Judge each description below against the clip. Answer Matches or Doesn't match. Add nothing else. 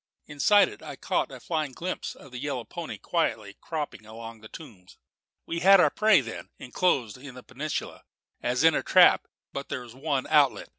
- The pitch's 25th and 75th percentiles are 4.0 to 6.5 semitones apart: Matches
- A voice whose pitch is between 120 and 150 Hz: Matches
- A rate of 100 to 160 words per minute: Doesn't match